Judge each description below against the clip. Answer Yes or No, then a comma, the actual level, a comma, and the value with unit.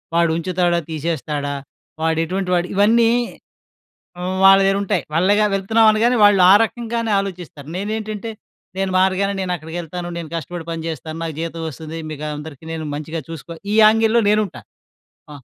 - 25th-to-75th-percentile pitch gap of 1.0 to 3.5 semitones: No, average, 4.1 semitones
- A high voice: No, medium, 180 Hz